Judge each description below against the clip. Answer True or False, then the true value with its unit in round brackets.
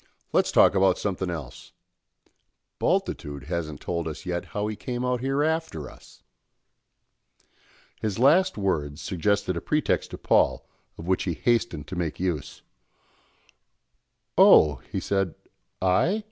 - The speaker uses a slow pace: True (130 wpm)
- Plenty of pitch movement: True (6.2 semitones)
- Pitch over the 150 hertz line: False (95 Hz)